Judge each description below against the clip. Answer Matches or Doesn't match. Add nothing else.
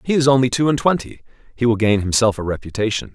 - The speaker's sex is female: Doesn't match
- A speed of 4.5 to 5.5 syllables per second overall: Doesn't match